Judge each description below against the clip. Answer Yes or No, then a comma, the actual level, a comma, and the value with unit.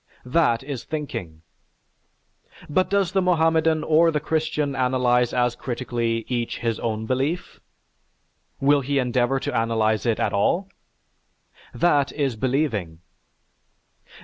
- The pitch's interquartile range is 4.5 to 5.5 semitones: Yes, average, 5.0 semitones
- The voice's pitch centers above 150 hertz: No, low, 130 Hz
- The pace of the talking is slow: Yes, slow, 120 wpm